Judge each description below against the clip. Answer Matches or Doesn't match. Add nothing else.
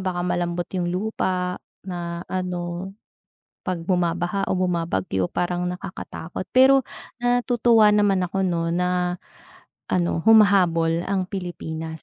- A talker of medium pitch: Matches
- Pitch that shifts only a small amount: Matches